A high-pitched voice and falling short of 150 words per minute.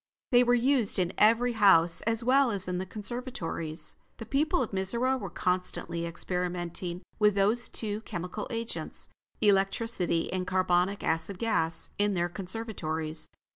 Yes: high, 195 Hz; average, 140 wpm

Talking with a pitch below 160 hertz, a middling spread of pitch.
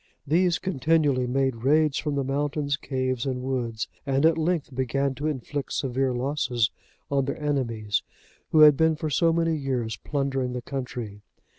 Yes: low, 135 Hz; average, 3.0 semitones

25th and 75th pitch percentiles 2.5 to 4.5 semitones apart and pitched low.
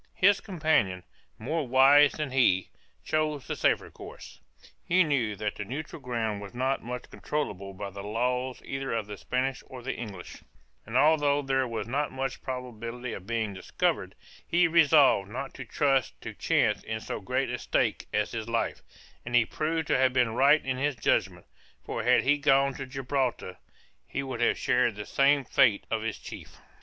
Yes: average, 3.8 semitones; low, 130 Hz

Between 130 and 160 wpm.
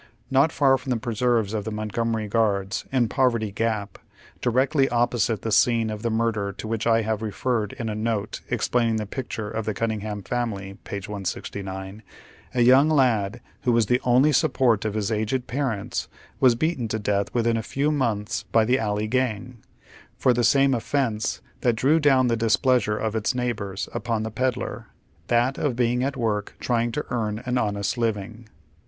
No: average, 185 wpm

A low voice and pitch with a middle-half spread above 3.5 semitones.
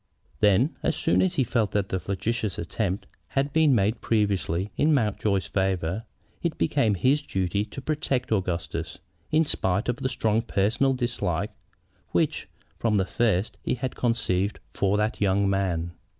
Yes: low, 105 Hz; average, 4.2 semitones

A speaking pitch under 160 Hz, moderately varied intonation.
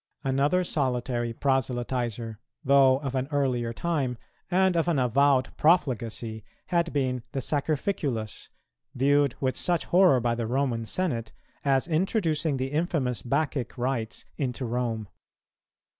Yes: low, 135 Hz; average, 3.7 semitones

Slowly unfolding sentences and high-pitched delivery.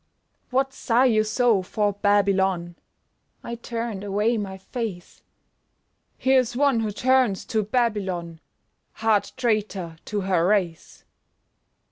Yes: slow, 110 wpm; high, 210 Hz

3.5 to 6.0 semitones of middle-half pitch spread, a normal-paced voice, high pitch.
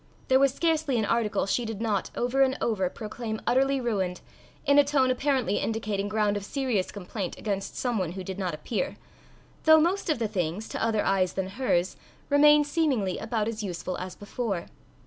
Yes: average, 5.3 semitones; average, 185 wpm; high, 220 Hz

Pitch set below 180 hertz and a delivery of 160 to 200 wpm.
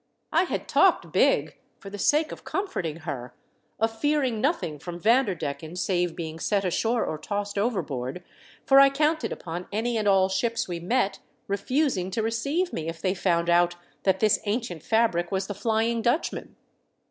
No: high, 200 Hz; average, 170 wpm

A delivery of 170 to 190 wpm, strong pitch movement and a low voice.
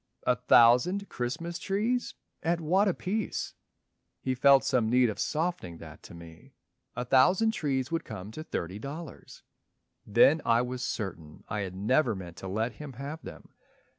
No: average, 160 wpm; wide, 7.1 semitones; low, 130 Hz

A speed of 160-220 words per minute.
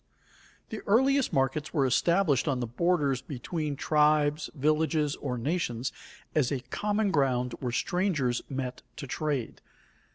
No: slow, 135 wpm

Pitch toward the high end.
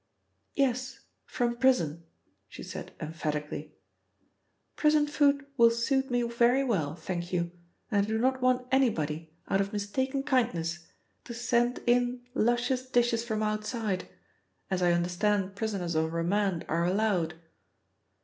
Yes: high, 220 Hz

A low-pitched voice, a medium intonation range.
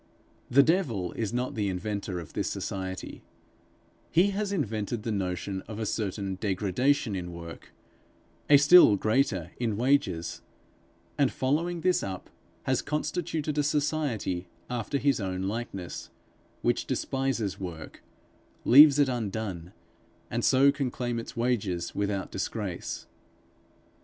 No: low, 115 Hz; wide, 6.6 semitones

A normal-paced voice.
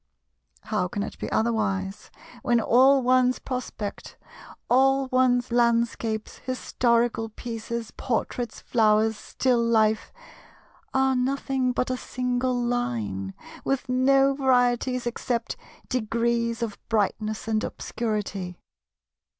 No: slow, 100 wpm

